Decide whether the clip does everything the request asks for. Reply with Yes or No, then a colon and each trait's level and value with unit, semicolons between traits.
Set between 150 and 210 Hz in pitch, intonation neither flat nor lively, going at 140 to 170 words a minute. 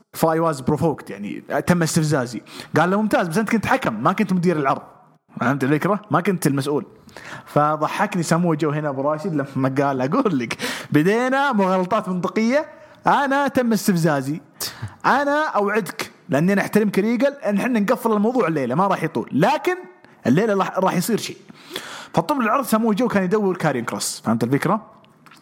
No: high, 190 Hz; wide, 6.3 semitones; average, 155 wpm